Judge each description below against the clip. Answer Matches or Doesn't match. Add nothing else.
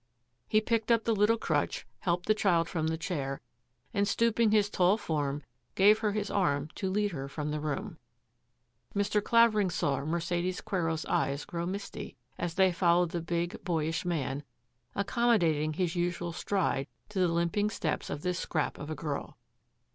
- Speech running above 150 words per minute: Matches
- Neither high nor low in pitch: Matches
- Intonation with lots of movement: Doesn't match